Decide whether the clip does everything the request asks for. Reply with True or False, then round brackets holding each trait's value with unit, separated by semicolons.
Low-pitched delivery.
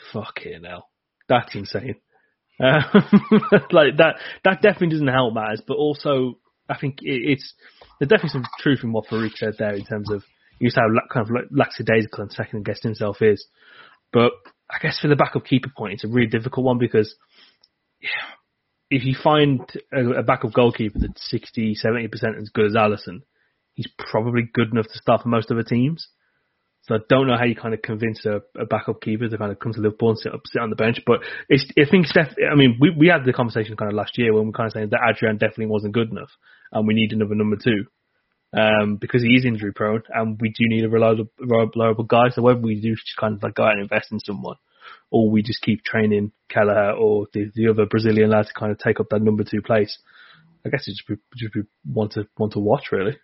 True (115 Hz)